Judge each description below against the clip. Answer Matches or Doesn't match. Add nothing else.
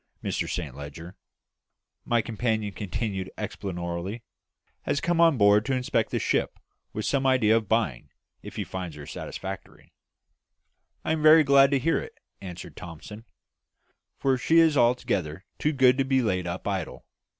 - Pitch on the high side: Doesn't match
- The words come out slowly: Doesn't match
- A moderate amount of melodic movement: Doesn't match